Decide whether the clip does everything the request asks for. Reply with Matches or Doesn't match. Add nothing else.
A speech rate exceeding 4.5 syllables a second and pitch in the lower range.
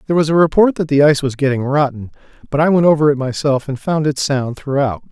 Doesn't match